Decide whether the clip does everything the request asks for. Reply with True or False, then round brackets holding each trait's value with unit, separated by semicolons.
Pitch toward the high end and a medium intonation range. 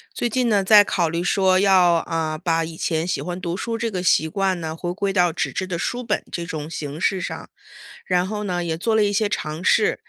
False (180 Hz; 3.5 semitones)